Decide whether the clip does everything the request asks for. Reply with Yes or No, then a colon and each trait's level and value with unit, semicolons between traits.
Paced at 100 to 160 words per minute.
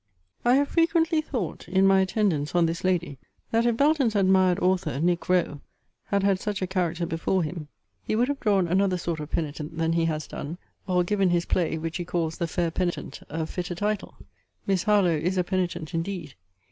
No: average, 195 wpm